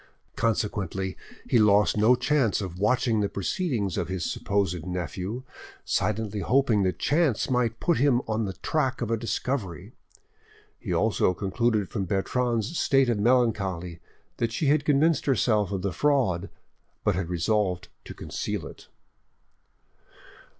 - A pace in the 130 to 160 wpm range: Yes, average, 140 wpm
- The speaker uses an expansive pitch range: No, average, 4.8 semitones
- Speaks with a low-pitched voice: Yes, low, 110 Hz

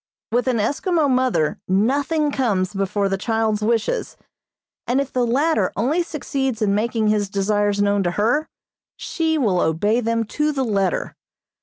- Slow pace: No, average, 155 wpm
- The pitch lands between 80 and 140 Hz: No, high, 225 Hz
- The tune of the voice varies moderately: Yes, average, 4.8 semitones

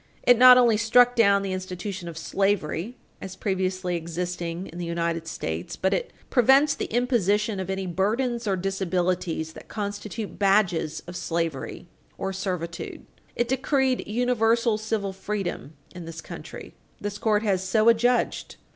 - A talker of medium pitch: No, high, 195 Hz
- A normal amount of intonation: Yes, average, 4.2 semitones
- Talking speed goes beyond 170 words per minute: No, average, 145 wpm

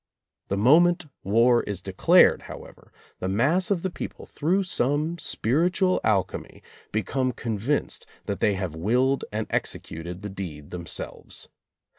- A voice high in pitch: No, low, 115 Hz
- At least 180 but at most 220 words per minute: No, average, 140 wpm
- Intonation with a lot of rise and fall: Yes, wide, 8.1 semitones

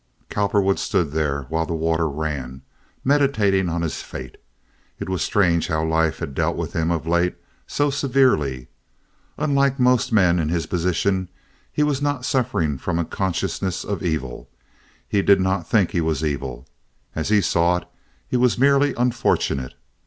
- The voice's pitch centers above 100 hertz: No, very low, 90 Hz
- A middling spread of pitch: No, wide, 6.3 semitones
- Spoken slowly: No, average, 160 wpm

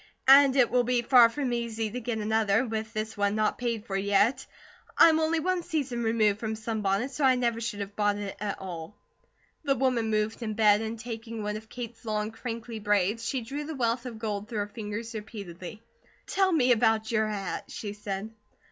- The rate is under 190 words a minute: No, average, 200 wpm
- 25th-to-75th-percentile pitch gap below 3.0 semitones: Yes, narrow, 2.6 semitones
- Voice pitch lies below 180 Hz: No, high, 225 Hz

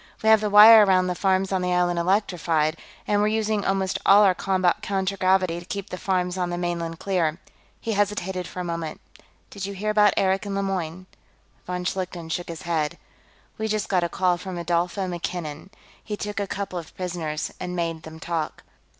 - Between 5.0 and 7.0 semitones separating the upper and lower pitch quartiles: No, narrow, 2.4 semitones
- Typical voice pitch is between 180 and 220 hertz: Yes, medium, 185 Hz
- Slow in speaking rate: No, average, 195 wpm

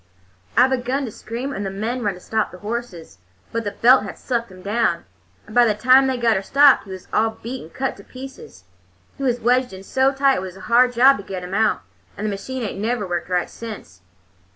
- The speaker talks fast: Yes, fast, 240 wpm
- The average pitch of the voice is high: Yes, high, 230 Hz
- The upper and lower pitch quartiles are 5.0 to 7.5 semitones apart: No, average, 4.6 semitones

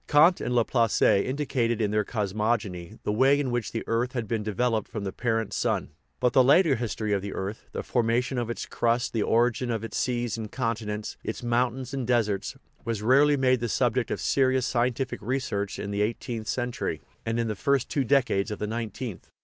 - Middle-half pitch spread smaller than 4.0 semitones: Yes, average, 2.9 semitones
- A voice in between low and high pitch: No, low, 120 Hz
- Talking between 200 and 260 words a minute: Yes, fast, 205 wpm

